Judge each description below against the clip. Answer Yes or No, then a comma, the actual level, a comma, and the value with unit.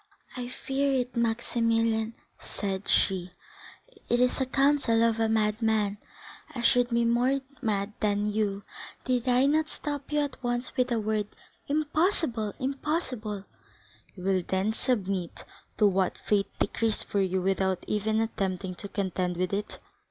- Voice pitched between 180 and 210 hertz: No, high, 225 Hz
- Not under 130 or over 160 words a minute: Yes, average, 150 wpm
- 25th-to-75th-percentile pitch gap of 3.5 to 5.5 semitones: Yes, average, 3.9 semitones